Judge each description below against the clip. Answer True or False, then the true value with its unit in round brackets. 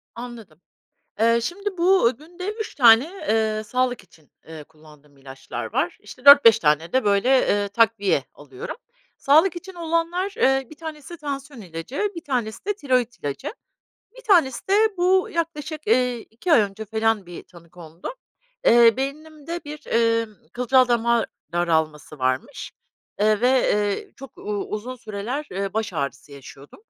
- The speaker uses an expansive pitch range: True (7.4 semitones)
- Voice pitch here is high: True (235 Hz)